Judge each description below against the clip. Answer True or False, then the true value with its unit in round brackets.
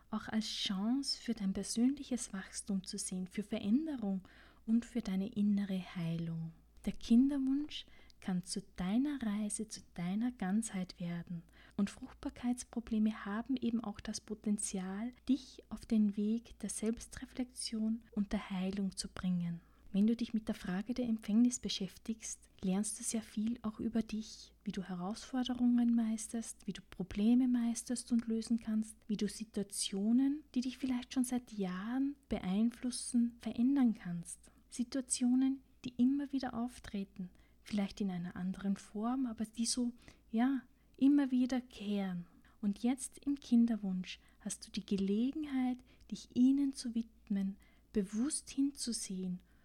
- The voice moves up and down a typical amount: True (3.6 semitones)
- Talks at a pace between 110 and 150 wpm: True (140 wpm)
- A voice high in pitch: True (225 Hz)